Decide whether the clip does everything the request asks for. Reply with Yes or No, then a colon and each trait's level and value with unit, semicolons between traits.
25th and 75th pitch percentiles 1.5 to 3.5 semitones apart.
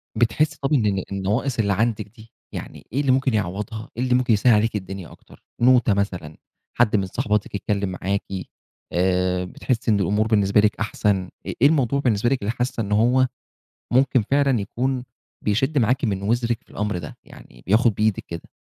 No: average, 3.9 semitones